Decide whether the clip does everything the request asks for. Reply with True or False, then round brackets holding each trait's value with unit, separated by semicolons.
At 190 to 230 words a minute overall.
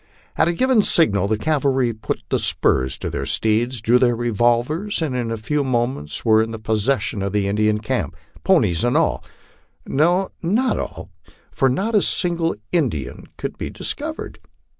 False (165 wpm)